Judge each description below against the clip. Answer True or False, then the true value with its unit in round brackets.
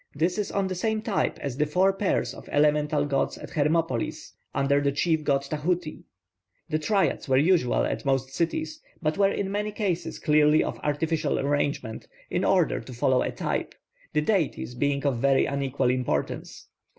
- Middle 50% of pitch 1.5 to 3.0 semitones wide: False (4.4 semitones)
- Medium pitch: True (150 Hz)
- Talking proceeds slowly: False (175 wpm)